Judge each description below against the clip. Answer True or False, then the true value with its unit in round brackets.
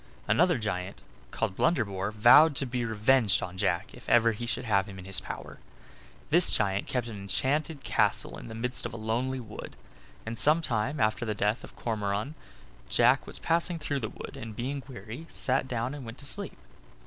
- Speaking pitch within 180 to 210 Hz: False (115 Hz)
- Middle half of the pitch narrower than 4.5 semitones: True (4.1 semitones)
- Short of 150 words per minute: False (195 wpm)